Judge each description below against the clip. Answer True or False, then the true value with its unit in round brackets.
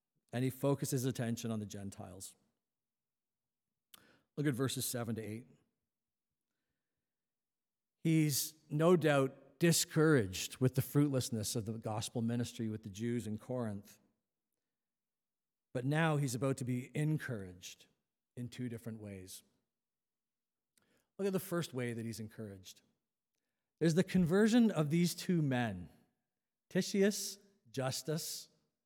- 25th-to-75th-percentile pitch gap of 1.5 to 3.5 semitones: False (5.4 semitones)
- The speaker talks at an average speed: False (120 wpm)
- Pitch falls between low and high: False (130 Hz)